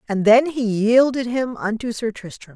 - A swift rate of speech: No, average, 190 wpm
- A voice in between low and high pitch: No, high, 230 Hz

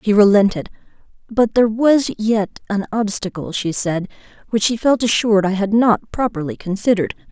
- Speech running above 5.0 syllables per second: Yes, 5.3 syllables/s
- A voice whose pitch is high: Yes, high, 210 Hz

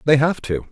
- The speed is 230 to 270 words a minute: Yes, fast, 250 wpm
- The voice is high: No, medium, 140 Hz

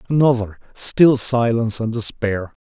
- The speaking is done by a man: Yes, male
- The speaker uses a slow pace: Yes, slow, 90 wpm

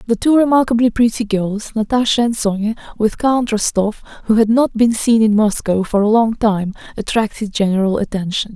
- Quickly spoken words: No, average, 175 wpm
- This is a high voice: Yes, high, 220 Hz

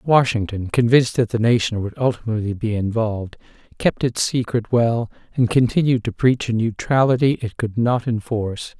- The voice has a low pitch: Yes, low, 115 Hz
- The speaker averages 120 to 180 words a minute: Yes, average, 155 wpm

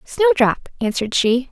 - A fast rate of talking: No, slow, 120 wpm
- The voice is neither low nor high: No, high, 235 Hz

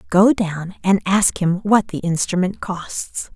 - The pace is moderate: Yes, average, 160 wpm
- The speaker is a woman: Yes, female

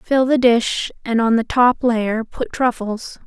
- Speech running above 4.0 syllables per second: No, 3.7 syllables/s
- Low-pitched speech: No, high, 235 Hz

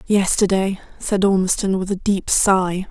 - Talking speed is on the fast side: No, average, 145 wpm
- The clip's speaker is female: Yes, female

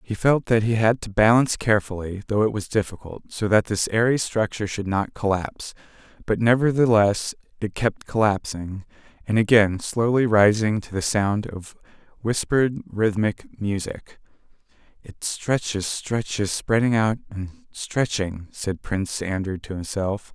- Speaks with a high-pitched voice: No, low, 105 Hz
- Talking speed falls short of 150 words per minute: Yes, average, 140 wpm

